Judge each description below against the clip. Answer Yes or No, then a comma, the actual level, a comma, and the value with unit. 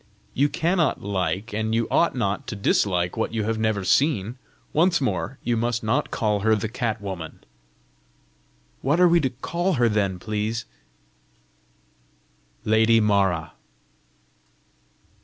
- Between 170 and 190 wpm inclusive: No, slow, 135 wpm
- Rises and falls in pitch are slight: No, average, 3.9 semitones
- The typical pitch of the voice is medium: No, low, 110 Hz